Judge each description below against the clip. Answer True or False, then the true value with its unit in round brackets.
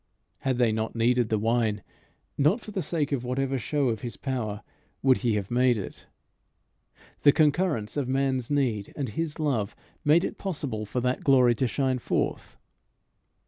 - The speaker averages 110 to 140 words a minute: False (170 wpm)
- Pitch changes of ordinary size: True (3.9 semitones)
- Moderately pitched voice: False (130 Hz)